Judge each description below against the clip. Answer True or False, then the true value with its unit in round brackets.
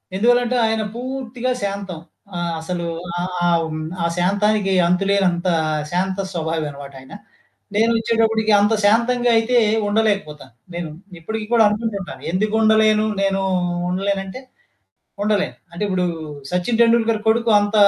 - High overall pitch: True (205 Hz)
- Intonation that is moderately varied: True (3.7 semitones)